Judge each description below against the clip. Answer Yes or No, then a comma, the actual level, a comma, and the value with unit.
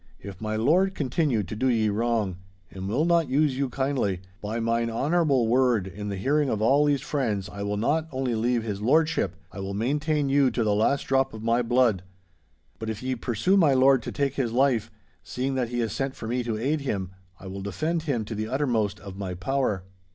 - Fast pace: Yes, fast, 215 wpm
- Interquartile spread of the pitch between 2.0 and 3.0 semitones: No, average, 4.6 semitones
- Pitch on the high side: No, low, 120 Hz